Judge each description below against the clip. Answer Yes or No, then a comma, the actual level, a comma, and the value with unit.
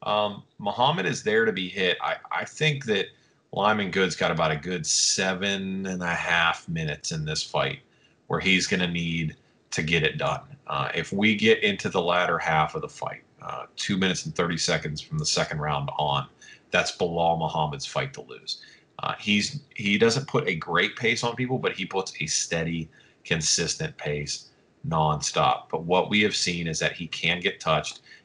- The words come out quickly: No, average, 195 wpm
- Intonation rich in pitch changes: Yes, wide, 5.9 semitones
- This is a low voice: Yes, very low, 95 Hz